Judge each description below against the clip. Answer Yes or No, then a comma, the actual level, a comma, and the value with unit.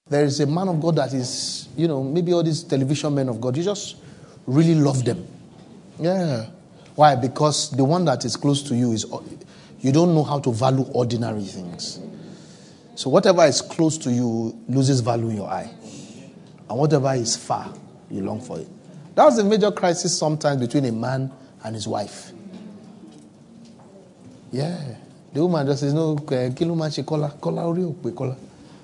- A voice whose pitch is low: No, medium, 145 Hz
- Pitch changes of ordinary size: Yes, average, 4.6 semitones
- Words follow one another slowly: No, average, 165 wpm